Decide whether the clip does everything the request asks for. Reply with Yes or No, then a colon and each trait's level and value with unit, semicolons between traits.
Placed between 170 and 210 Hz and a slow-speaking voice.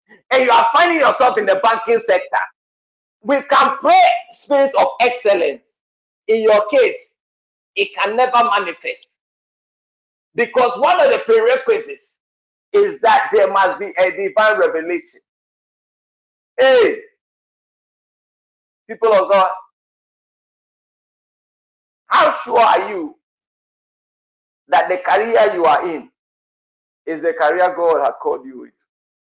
No: very high, 280 Hz; slow, 115 wpm